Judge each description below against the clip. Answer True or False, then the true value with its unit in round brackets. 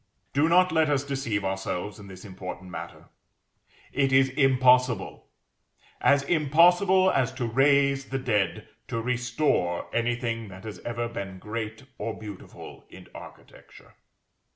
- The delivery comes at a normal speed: False (130 wpm)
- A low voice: True (125 Hz)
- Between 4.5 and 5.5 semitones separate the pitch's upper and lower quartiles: True (4.8 semitones)